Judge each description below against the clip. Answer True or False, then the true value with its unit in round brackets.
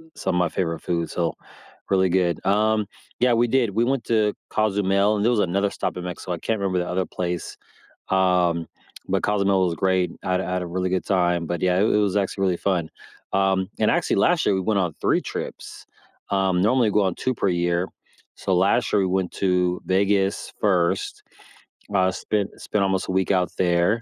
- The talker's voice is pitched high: False (95 Hz)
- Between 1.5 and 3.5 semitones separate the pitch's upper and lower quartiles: True (2.4 semitones)